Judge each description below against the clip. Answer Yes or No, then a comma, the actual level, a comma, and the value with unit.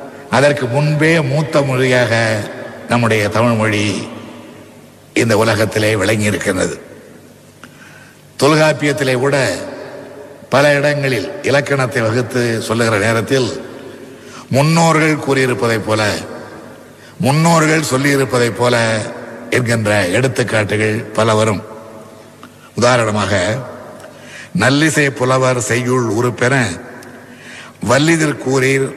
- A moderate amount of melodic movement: Yes, average, 3.8 semitones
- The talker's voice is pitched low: Yes, low, 125 Hz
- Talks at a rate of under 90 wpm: Yes, slow, 75 wpm